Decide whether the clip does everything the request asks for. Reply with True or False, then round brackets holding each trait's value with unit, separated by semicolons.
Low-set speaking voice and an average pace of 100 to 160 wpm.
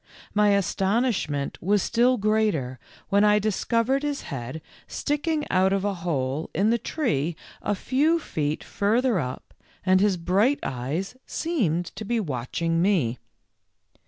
False (200 Hz; 140 wpm)